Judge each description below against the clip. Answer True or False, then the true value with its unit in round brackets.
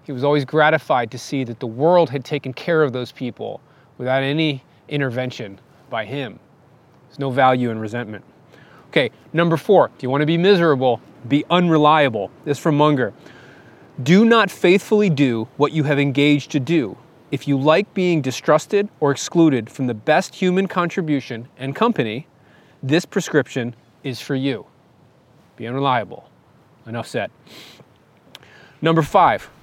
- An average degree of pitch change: True (3.8 semitones)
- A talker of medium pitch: True (145 Hz)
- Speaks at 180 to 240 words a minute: False (150 wpm)